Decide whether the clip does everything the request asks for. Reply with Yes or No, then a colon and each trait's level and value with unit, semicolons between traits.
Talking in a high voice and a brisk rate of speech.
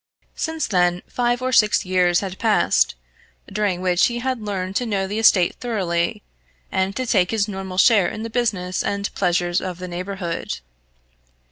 No: high, 195 Hz; average, 165 wpm